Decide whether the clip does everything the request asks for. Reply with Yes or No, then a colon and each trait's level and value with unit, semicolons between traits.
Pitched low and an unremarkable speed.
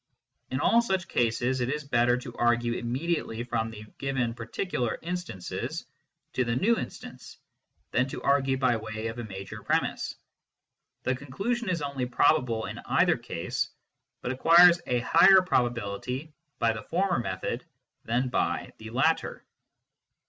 Yes: low, 125 Hz; average, 145 wpm